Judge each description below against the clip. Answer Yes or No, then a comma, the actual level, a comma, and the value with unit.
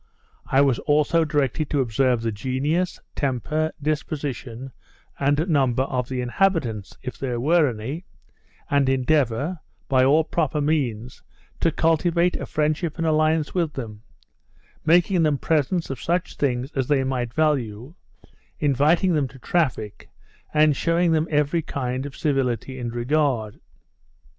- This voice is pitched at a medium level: Yes, medium, 145 Hz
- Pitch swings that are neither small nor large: Yes, average, 3.8 semitones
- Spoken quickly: No, average, 140 wpm